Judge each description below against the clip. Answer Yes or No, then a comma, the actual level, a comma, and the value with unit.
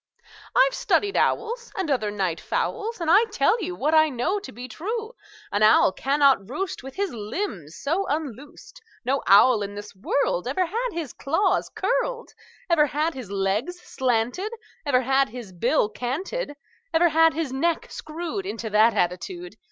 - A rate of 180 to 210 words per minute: No, average, 165 wpm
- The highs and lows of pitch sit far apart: Yes, wide, 8.1 semitones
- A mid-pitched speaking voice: No, very high, 290 Hz